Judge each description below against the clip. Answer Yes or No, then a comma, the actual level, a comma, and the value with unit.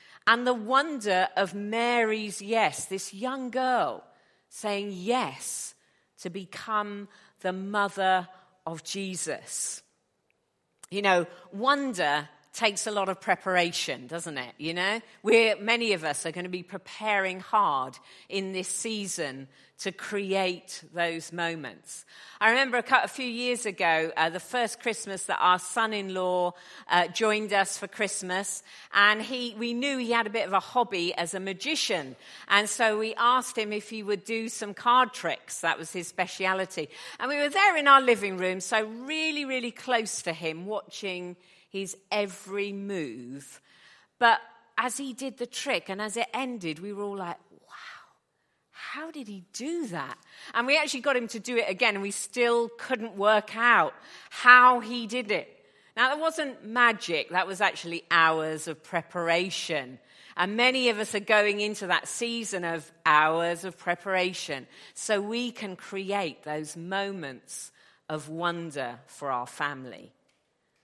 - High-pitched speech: Yes, high, 200 Hz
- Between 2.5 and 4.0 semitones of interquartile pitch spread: No, average, 4.7 semitones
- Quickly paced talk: No, average, 160 wpm